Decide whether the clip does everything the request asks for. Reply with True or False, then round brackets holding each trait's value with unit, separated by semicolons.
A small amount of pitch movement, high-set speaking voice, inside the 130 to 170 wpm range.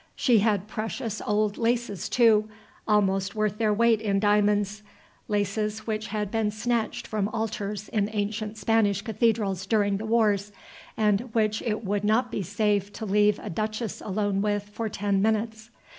True (1.3 semitones; 210 Hz; 160 wpm)